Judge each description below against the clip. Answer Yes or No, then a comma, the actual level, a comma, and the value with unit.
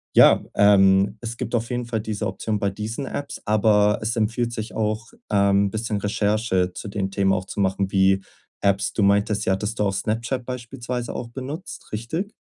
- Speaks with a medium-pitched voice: No, low, 105 Hz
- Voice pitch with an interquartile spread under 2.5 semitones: No, average, 2.8 semitones